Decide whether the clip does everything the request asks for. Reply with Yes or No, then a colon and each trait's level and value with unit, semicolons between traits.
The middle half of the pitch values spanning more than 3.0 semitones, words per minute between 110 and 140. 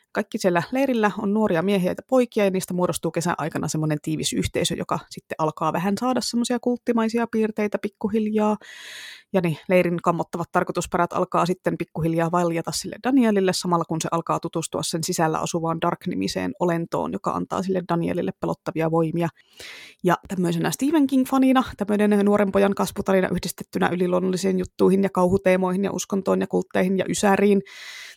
No: average, 3.5 semitones; average, 150 wpm